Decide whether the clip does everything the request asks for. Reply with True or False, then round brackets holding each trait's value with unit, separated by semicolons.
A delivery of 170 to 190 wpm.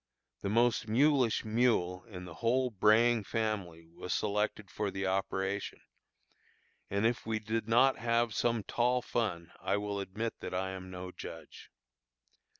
False (150 wpm)